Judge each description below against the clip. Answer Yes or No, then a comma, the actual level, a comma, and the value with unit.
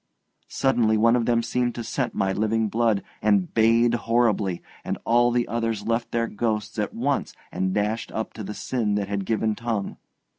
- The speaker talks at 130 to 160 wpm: No, average, 185 wpm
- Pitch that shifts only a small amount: Yes, narrow, 2.1 semitones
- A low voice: Yes, low, 115 Hz